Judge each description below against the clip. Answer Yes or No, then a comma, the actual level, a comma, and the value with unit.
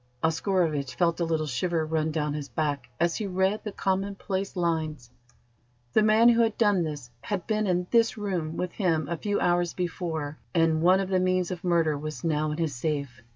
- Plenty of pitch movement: No, average, 3.5 semitones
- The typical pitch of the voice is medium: Yes, medium, 170 Hz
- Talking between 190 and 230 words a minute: Yes, average, 200 wpm